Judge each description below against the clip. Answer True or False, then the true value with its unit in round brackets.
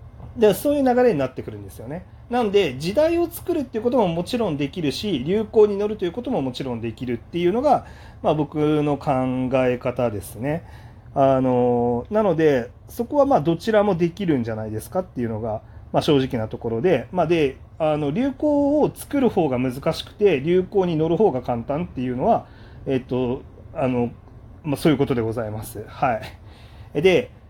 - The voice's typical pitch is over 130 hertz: True (140 Hz)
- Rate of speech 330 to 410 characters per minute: True (365 characters per minute)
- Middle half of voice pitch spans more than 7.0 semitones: True (8.9 semitones)